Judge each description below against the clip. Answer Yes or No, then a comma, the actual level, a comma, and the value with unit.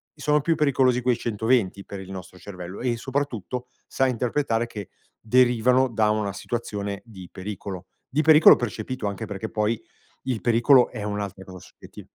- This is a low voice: Yes, low, 115 Hz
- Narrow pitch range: No, average, 3.9 semitones